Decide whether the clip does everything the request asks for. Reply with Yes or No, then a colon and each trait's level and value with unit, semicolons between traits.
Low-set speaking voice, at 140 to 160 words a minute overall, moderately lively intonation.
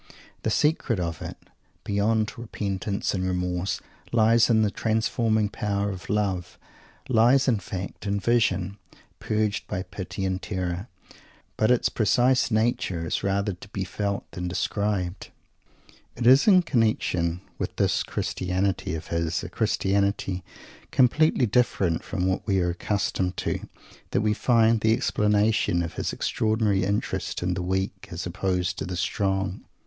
Yes: low, 100 Hz; average, 145 wpm; average, 3.1 semitones